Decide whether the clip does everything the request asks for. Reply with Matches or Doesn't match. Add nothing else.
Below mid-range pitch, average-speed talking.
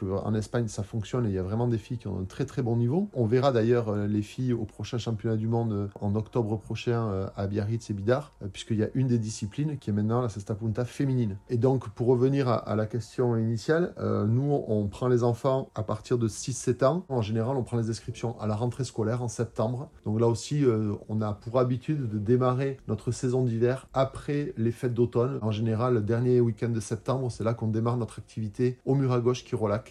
Doesn't match